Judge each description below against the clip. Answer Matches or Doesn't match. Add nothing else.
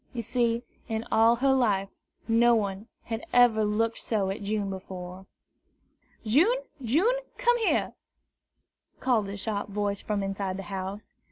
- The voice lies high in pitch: Matches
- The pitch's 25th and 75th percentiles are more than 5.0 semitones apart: Doesn't match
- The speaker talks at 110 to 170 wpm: Matches